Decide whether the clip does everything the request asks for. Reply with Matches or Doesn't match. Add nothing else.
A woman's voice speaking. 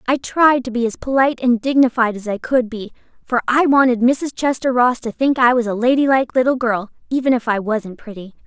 Matches